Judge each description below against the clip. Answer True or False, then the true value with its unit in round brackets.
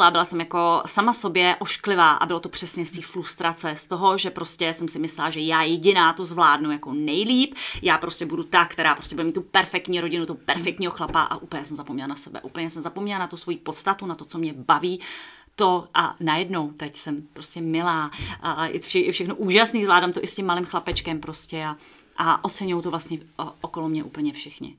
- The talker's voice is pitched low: False (170 Hz)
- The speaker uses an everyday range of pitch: False (2.3 semitones)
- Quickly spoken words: True (220 wpm)